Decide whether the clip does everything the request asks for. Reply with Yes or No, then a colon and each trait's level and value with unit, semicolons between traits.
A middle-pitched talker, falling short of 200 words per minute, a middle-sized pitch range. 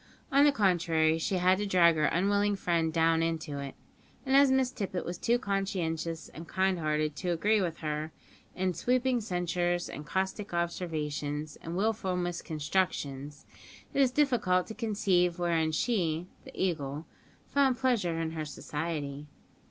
Yes: medium, 175 Hz; average, 155 wpm; average, 4.0 semitones